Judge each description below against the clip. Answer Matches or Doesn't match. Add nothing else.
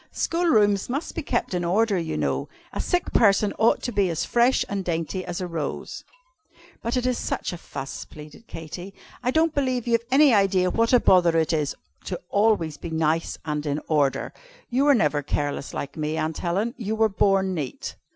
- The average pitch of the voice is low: Doesn't match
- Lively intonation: Matches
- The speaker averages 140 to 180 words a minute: Doesn't match